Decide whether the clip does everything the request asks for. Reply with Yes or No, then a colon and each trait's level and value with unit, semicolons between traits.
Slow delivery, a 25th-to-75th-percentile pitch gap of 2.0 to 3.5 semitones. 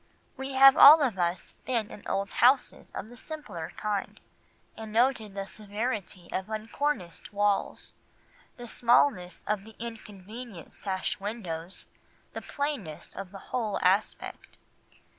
No: slow, 130 wpm; average, 4.0 semitones